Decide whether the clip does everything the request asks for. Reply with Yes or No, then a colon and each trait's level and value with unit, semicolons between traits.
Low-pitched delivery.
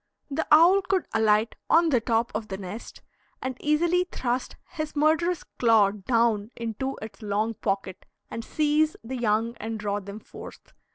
No: high, 230 Hz